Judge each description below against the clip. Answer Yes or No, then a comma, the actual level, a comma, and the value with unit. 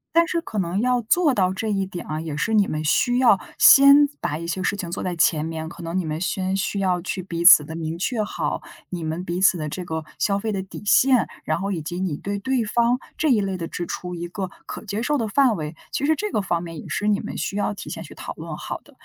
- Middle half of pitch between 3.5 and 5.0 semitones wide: Yes, average, 4.6 semitones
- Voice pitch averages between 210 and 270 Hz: No, high, 190 Hz